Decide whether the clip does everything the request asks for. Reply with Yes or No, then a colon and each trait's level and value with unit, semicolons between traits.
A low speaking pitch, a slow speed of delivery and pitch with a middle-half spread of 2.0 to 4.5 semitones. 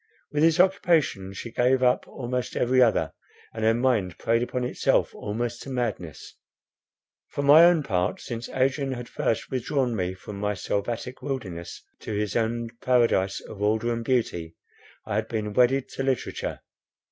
No: low, 120 Hz; average, 160 wpm; average, 3.7 semitones